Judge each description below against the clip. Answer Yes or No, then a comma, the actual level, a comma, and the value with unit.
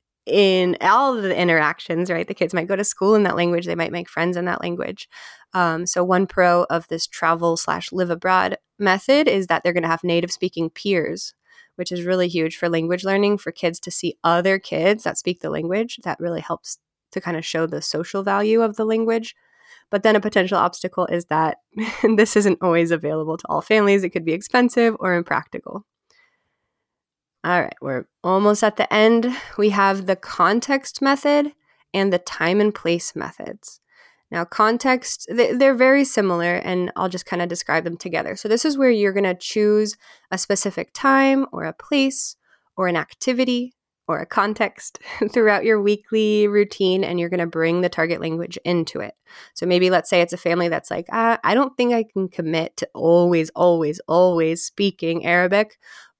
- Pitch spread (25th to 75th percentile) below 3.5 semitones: No, average, 4.1 semitones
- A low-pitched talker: No, medium, 185 Hz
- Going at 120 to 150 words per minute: No, average, 185 wpm